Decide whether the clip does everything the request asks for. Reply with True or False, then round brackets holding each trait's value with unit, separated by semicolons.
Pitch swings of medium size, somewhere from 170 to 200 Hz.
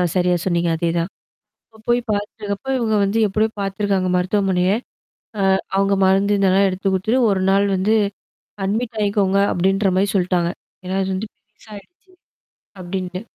False (1.9 semitones; 195 Hz)